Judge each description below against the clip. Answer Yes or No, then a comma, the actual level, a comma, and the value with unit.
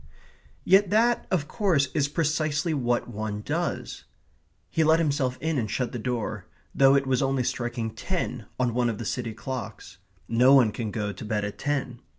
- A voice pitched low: Yes, low, 130 Hz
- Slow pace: No, average, 180 wpm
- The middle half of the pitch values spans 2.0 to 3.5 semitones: No, average, 4.5 semitones